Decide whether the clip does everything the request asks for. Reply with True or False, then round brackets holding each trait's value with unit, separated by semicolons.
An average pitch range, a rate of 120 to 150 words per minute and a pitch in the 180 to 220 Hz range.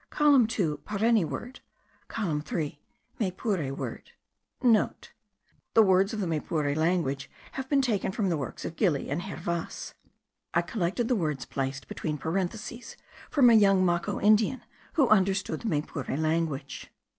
False (5.8 semitones; 145 wpm; 185 Hz)